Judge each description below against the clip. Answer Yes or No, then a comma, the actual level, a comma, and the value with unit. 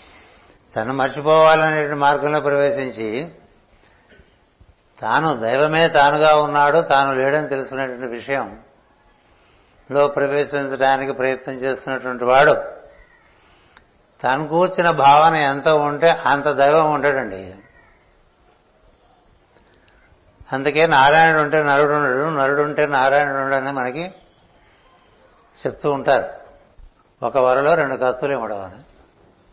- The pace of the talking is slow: No, average, 85 wpm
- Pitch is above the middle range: No, medium, 140 Hz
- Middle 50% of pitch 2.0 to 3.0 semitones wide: Yes, narrow, 2.5 semitones